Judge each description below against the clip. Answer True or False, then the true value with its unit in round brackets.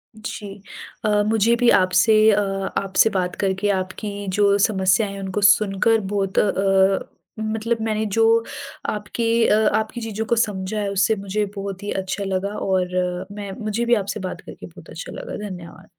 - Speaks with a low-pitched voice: False (205 Hz)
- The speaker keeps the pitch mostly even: True (2.2 semitones)